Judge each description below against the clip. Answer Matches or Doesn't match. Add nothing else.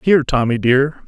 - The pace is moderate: Matches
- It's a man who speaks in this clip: Matches